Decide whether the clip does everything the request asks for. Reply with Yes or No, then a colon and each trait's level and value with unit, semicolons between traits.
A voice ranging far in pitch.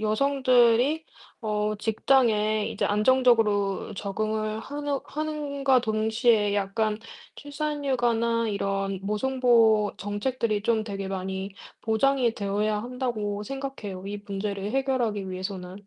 No: average, 3.9 semitones